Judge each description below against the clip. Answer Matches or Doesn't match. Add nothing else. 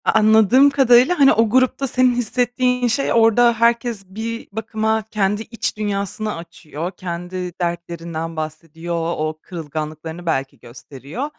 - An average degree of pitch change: Doesn't match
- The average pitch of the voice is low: Doesn't match